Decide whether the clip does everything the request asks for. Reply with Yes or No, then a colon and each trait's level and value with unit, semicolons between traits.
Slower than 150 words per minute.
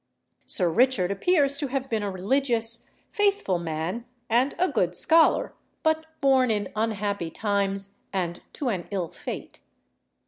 Yes: average, 140 wpm